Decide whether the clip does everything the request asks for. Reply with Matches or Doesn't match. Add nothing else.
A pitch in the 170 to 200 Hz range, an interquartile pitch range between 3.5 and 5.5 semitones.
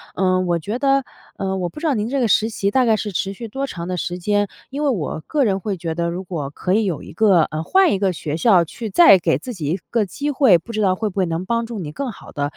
Matches